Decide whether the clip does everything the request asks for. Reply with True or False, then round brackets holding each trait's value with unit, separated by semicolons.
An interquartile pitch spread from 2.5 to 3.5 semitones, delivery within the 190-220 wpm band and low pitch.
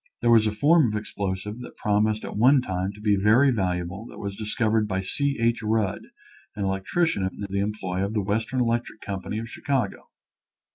True (2.9 semitones; 195 wpm; 105 Hz)